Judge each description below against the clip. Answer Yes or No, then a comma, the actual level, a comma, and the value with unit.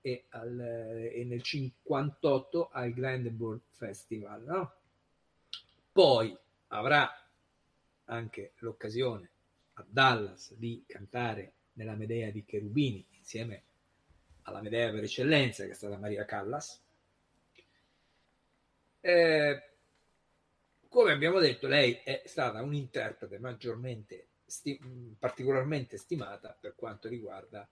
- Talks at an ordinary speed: No, slow, 100 wpm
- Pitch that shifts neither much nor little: Yes, average, 3.8 semitones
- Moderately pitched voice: No, low, 115 Hz